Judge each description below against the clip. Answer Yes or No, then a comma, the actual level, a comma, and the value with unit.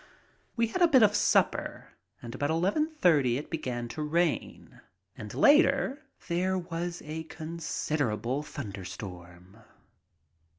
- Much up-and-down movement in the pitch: Yes, wide, 7.4 semitones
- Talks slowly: Yes, slow, 120 wpm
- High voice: No, medium, 160 Hz